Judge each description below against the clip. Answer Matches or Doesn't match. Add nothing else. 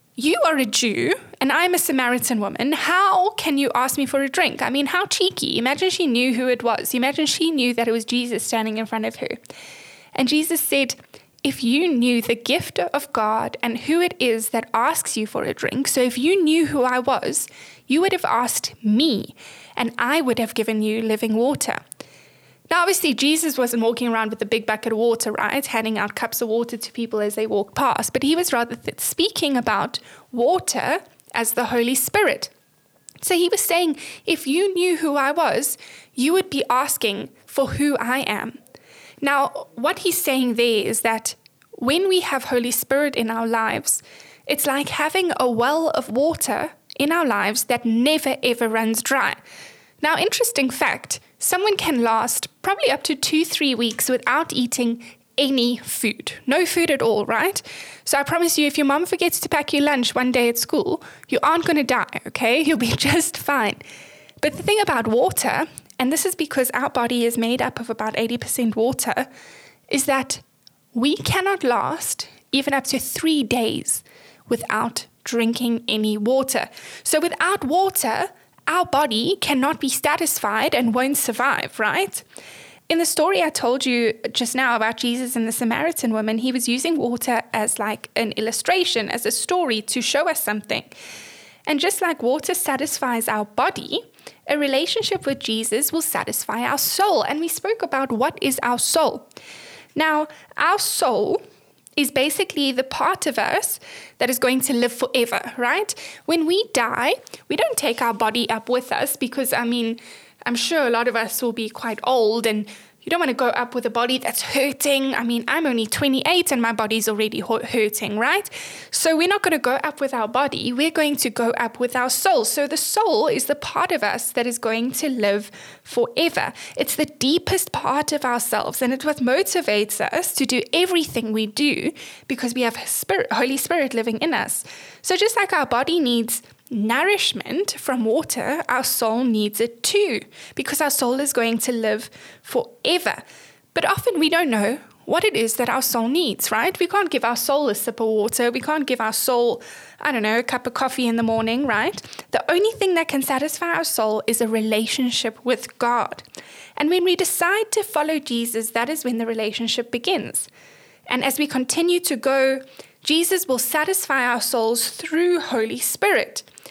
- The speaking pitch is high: Matches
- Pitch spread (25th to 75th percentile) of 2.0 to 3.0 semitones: Doesn't match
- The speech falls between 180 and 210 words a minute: Matches